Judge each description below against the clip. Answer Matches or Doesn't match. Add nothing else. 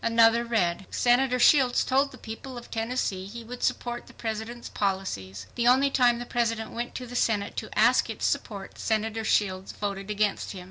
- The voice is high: Matches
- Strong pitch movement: Doesn't match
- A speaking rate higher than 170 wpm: Matches